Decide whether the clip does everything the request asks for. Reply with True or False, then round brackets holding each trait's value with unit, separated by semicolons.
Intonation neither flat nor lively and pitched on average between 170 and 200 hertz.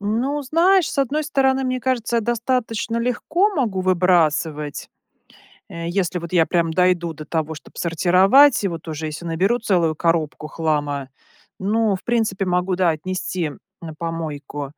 False (6.3 semitones; 185 Hz)